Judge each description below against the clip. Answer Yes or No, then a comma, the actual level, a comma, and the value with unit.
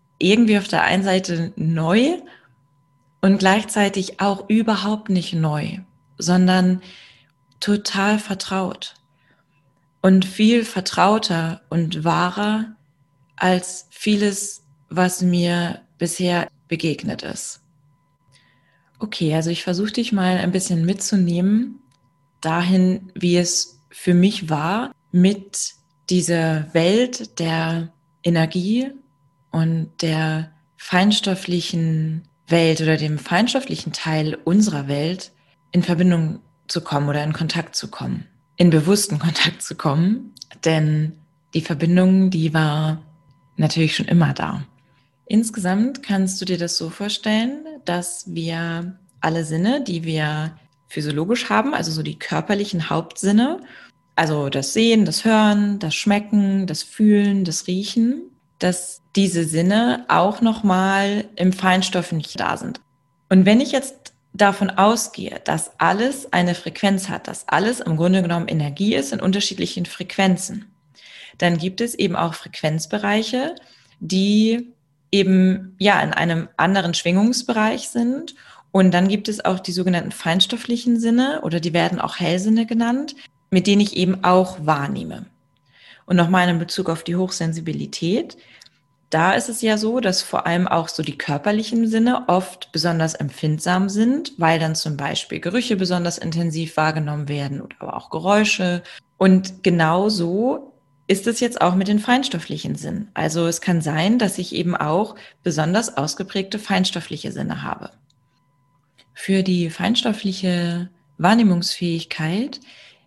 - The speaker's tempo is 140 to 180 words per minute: No, average, 130 wpm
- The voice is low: No, medium, 180 Hz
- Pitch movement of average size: Yes, average, 3.9 semitones